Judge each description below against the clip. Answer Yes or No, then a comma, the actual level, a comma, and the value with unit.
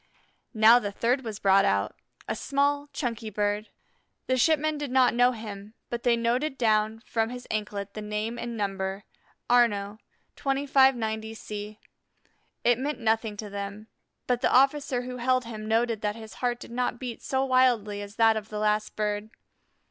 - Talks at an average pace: Yes, average, 170 wpm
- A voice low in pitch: No, high, 225 Hz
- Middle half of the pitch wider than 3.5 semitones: No, average, 3.0 semitones